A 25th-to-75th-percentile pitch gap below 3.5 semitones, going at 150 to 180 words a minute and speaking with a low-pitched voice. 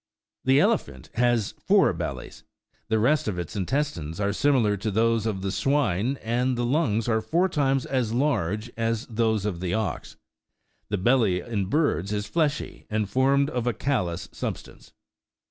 No: average, 4.7 semitones; average, 165 wpm; low, 115 Hz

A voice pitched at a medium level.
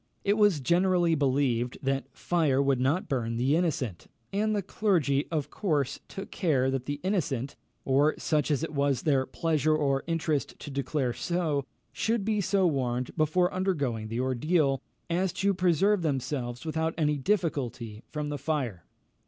Yes: medium, 150 Hz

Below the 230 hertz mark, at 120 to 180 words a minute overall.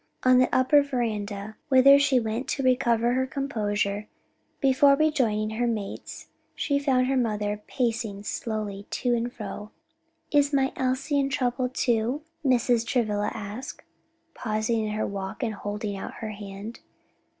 No: high, 235 Hz; average, 145 wpm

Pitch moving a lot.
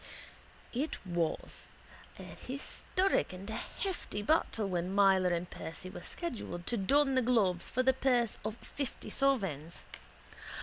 Yes: wide, 6.3 semitones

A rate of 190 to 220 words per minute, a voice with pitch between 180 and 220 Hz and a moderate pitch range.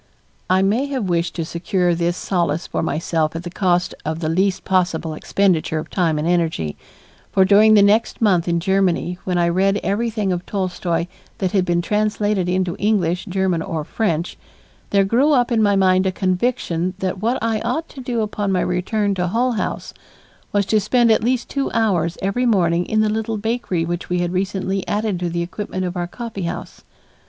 Yes: average, 195 wpm; high, 190 Hz; average, 3.5 semitones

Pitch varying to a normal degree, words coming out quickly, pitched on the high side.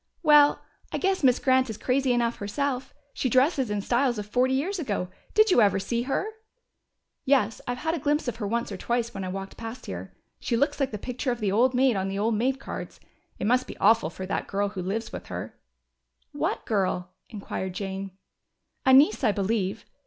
Yes: average, 4.6 semitones; fast, 210 wpm; high, 235 Hz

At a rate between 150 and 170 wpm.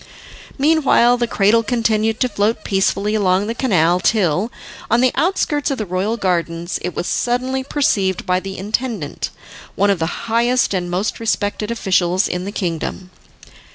Yes: average, 155 wpm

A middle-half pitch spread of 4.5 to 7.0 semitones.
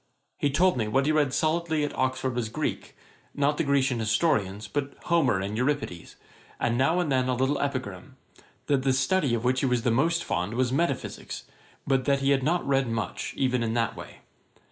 No: average, 3.4 semitones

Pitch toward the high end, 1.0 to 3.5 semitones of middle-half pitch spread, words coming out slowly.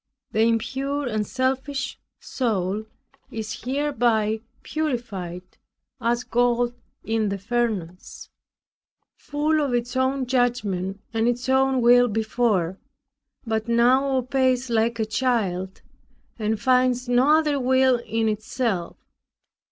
Yes: high, 240 Hz; average, 3.1 semitones; slow, 110 wpm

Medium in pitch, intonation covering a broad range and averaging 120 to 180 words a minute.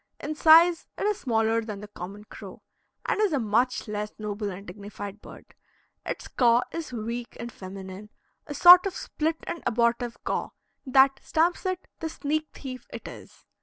No: high, 240 Hz; wide, 6.9 semitones; average, 170 wpm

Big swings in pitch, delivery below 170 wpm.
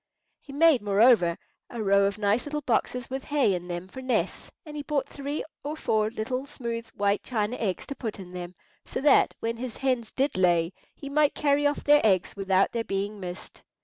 No: wide, 6.0 semitones; fast, 205 wpm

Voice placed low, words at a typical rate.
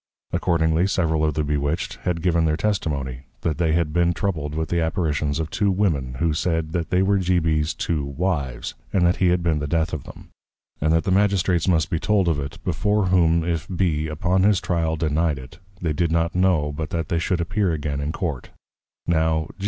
No: very low, 80 Hz; fast, 210 wpm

